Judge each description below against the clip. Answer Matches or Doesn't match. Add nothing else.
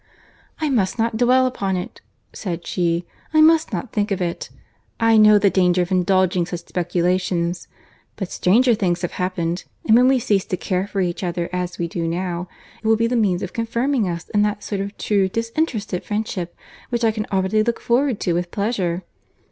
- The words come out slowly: Doesn't match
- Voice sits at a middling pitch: Doesn't match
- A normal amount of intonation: Matches